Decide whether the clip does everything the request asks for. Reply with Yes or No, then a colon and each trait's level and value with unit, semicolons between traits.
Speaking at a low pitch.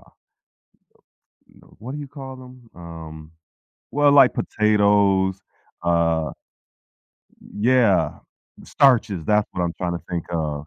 Yes: low, 100 Hz